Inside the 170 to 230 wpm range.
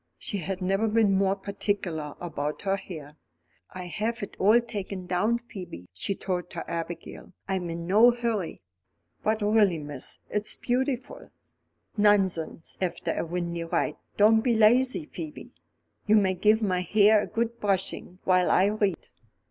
No: average, 155 wpm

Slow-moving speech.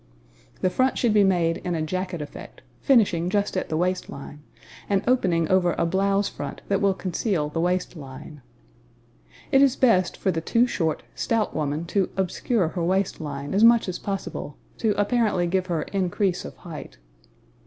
No: average, 175 wpm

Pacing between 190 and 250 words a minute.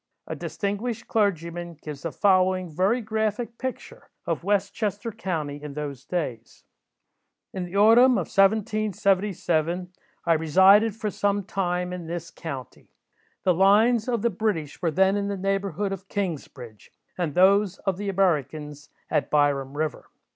No: average, 145 wpm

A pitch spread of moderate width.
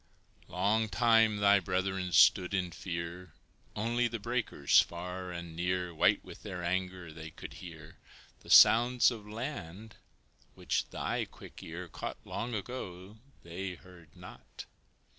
Yes: average, 3.9 semitones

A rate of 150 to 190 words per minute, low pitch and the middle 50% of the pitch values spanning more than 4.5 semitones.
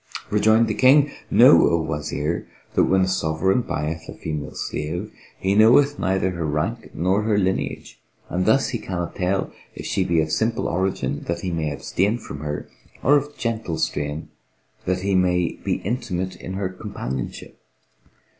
Yes: average, 165 wpm; very low, 95 Hz; average, 4.9 semitones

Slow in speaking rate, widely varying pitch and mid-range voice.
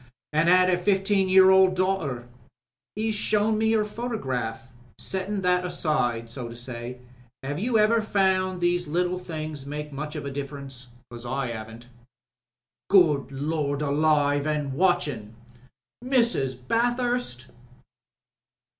Yes: slow, 120 wpm; wide, 6.0 semitones; medium, 155 Hz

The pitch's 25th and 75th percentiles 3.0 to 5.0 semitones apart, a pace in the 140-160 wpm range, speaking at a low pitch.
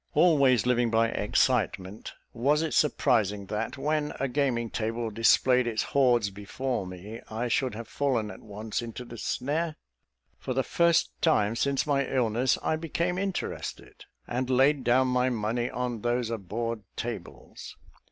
Yes: average, 3.5 semitones; average, 150 wpm; low, 125 Hz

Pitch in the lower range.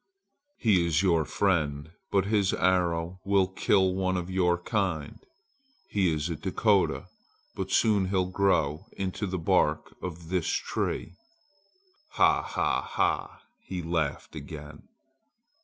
Yes: very low, 90 Hz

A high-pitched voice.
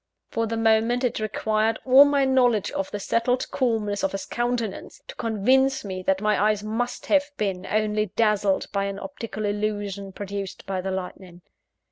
Yes: high, 215 Hz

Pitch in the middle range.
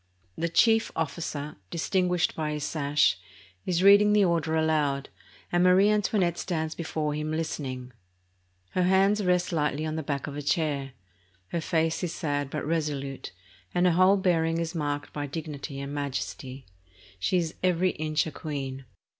Yes: medium, 160 Hz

